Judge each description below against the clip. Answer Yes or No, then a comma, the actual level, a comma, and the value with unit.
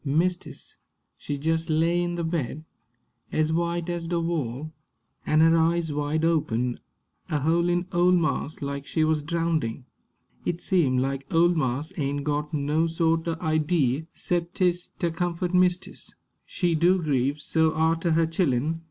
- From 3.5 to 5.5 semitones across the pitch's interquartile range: No, narrow, 2.5 semitones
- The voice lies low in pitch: No, medium, 160 Hz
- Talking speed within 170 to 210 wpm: No, average, 150 wpm